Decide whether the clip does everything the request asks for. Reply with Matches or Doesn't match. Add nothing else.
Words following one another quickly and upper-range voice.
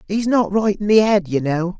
Matches